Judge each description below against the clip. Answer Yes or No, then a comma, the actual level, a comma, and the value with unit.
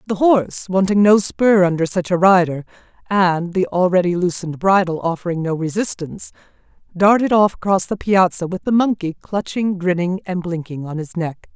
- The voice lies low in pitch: No, medium, 185 Hz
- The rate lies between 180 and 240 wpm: No, average, 165 wpm